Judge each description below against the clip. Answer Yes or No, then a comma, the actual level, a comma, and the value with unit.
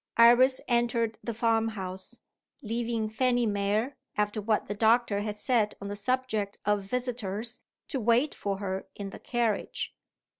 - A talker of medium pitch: No, high, 225 Hz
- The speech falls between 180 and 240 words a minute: No, average, 150 wpm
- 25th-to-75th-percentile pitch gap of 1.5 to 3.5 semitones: Yes, average, 2.7 semitones